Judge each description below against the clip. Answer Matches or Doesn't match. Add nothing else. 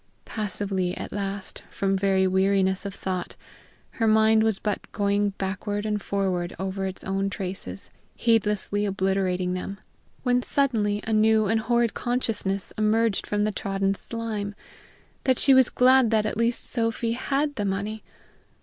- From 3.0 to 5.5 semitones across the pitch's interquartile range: Doesn't match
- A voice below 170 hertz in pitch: Doesn't match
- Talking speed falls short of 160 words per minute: Matches